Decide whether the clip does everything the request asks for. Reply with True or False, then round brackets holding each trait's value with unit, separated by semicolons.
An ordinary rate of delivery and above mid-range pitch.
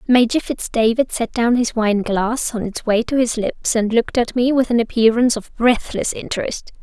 False (210 wpm; 235 Hz)